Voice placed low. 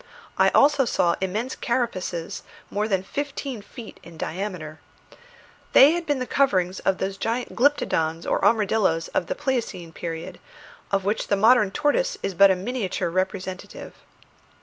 No: high, 200 Hz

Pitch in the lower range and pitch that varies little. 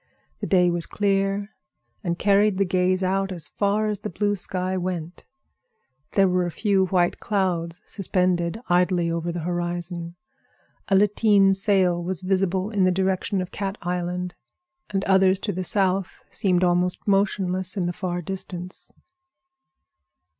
No: medium, 185 Hz; narrow, 1.8 semitones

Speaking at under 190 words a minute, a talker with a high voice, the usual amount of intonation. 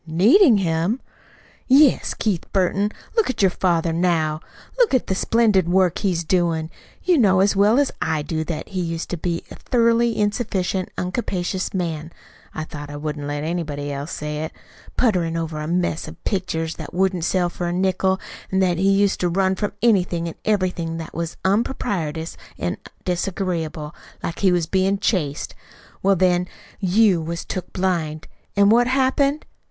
No: average, 170 wpm; medium, 180 Hz; average, 3.4 semitones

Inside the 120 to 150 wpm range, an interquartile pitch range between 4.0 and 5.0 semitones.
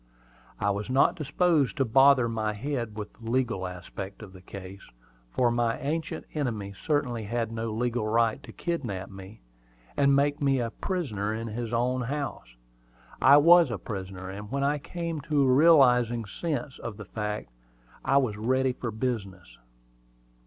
No: average, 165 wpm; average, 4.7 semitones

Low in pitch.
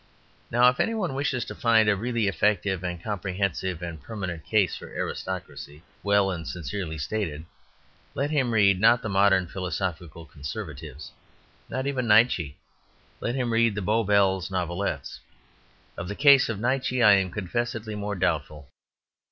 Yes: low, 100 Hz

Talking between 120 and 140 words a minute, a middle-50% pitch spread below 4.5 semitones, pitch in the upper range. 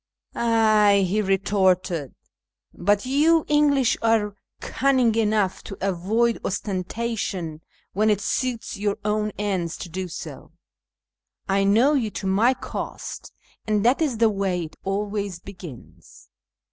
Yes: slow, 135 wpm; average, 3.1 semitones; high, 205 Hz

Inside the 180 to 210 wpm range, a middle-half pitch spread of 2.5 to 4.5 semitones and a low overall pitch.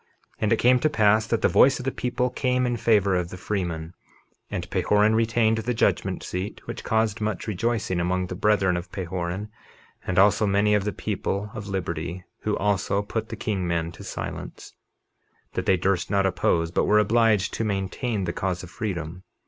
Yes: average, 190 wpm; average, 3.3 semitones; low, 100 Hz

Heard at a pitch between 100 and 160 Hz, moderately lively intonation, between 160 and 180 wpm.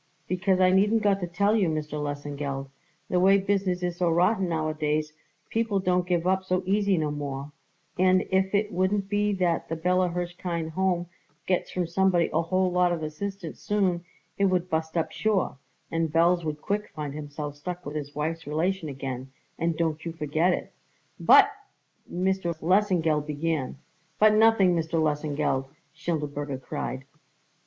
No: medium, 175 Hz; average, 3.6 semitones; average, 165 wpm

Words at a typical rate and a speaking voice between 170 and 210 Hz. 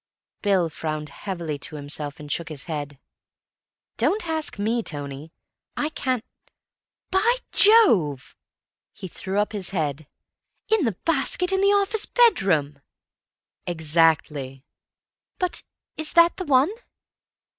No: slow, 115 wpm; high, 190 Hz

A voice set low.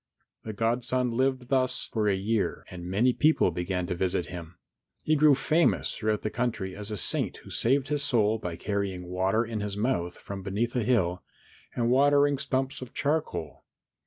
Yes: low, 110 Hz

